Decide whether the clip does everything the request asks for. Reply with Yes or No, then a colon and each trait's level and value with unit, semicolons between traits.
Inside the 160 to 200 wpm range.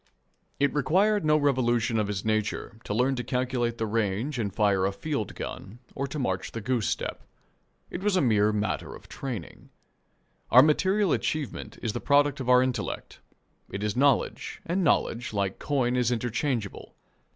Yes: average, 170 wpm